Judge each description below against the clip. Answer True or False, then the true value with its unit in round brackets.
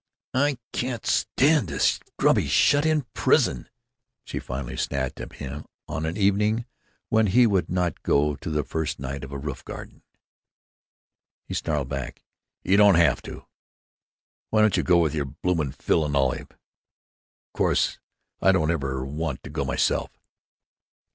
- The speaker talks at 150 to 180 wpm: True (155 wpm)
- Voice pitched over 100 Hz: False (80 Hz)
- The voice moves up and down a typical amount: False (6.8 semitones)